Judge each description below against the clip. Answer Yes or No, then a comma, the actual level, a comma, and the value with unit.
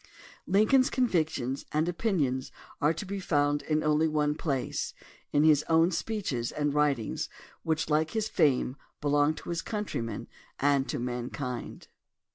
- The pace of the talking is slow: No, average, 145 wpm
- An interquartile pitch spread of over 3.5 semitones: No, average, 3.2 semitones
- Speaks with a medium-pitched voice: Yes, medium, 150 Hz